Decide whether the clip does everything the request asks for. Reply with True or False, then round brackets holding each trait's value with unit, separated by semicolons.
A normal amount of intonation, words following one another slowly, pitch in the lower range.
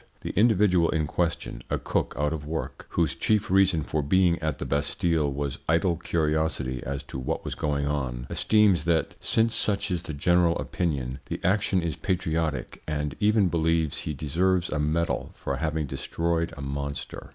False (3.4 semitones; 175 wpm; 80 Hz)